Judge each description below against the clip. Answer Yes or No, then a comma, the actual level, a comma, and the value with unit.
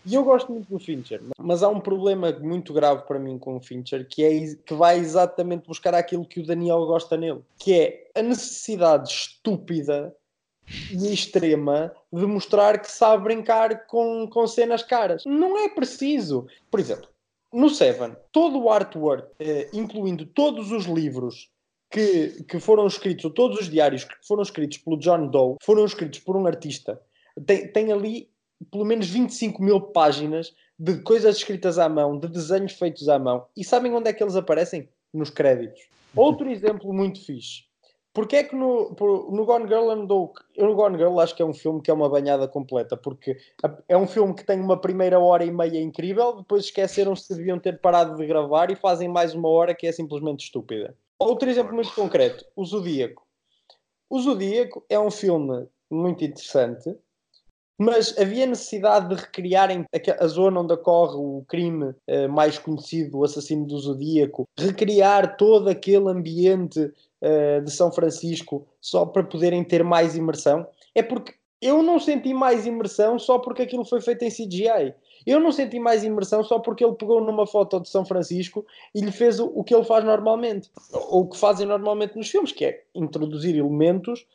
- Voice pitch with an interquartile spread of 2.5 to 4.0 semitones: No, wide, 5.4 semitones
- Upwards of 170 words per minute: Yes, average, 180 wpm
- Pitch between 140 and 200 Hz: Yes, high, 190 Hz